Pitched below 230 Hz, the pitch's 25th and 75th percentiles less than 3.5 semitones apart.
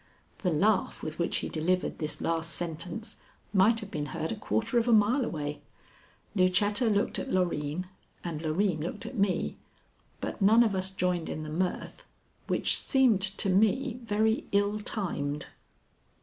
No: high, 190 Hz; average, 4.6 semitones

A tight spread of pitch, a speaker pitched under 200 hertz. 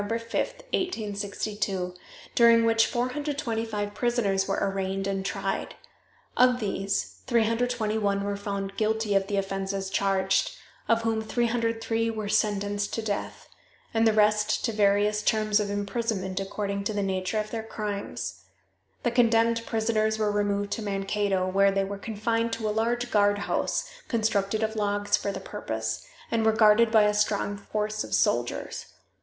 No: narrow, 2.2 semitones; high, 210 Hz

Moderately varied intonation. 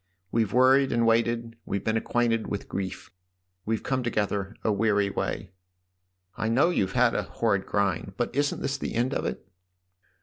Yes: average, 3.3 semitones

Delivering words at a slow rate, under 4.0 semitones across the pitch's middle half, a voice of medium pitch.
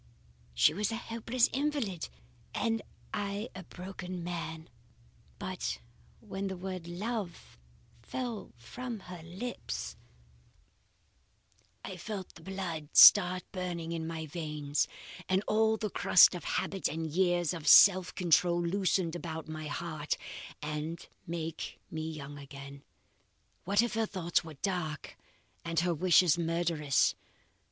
Yes: slow, 125 wpm; average, 3.4 semitones; medium, 175 Hz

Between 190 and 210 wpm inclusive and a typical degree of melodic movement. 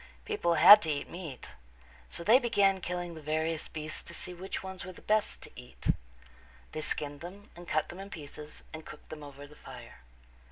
Yes: average, 200 wpm; average, 3.7 semitones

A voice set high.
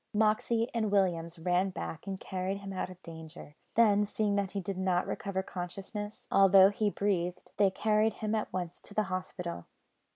Yes: high, 195 Hz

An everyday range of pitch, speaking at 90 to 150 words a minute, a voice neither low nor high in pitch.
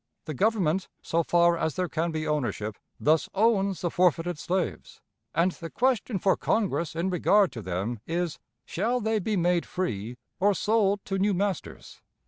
No: average, 3.8 semitones; average, 165 wpm; medium, 180 Hz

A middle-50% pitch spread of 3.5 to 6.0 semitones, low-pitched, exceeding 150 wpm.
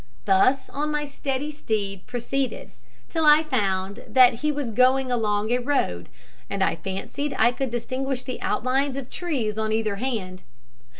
No: average, 4.4 semitones; very high, 255 Hz; average, 160 wpm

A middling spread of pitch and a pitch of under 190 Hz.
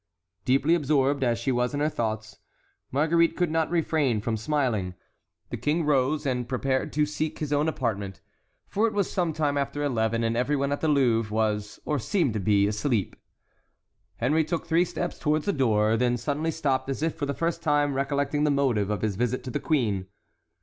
Yes: average, 4.8 semitones; medium, 140 Hz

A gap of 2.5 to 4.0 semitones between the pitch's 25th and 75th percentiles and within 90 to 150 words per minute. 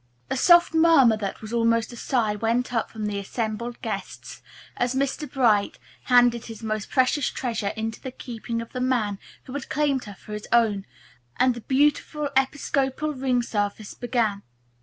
No: average, 3.4 semitones; average, 170 wpm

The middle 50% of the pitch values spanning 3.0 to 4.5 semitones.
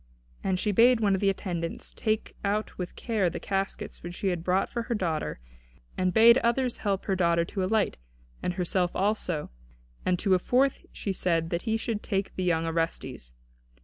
Yes: average, 3.6 semitones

